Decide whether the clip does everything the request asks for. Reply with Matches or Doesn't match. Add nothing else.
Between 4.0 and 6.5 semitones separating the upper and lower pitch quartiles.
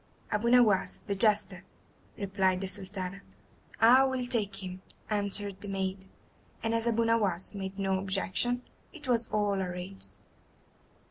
Doesn't match